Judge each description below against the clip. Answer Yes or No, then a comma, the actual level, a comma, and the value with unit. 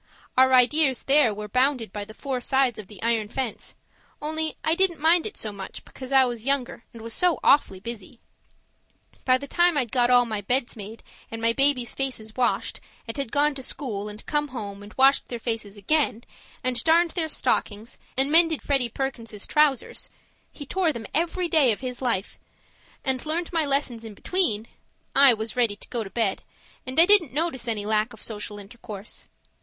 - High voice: Yes, very high, 250 Hz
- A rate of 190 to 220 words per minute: Yes, average, 195 wpm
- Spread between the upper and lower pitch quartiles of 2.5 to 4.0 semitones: No, average, 4.7 semitones